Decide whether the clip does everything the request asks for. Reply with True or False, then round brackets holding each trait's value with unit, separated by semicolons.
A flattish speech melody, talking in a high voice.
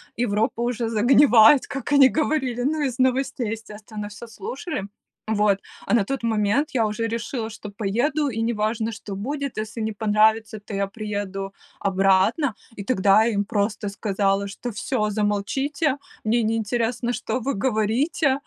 False (3.3 semitones; 225 Hz)